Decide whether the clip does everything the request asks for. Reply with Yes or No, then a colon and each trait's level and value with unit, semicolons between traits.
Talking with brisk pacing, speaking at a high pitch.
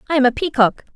Yes: fast, 250 wpm; very high, 265 Hz